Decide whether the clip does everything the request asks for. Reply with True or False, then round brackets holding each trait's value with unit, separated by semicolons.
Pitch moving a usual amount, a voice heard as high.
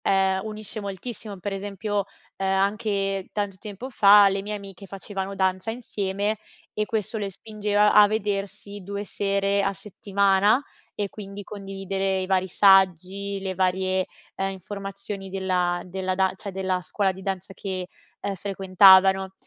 False (1.2 semitones; 195 Hz)